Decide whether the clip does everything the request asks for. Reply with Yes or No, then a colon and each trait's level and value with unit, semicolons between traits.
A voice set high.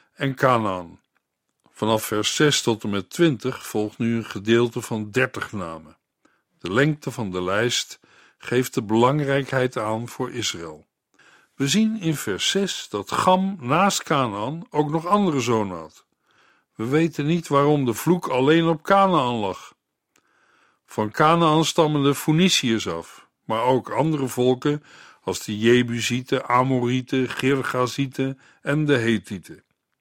No: low, 130 Hz